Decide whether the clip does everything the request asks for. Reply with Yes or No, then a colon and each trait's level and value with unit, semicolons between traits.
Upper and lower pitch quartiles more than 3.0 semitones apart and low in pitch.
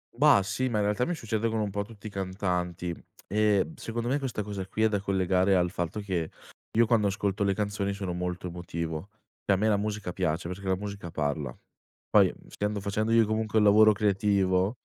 No: narrow, 2.6 semitones; low, 100 Hz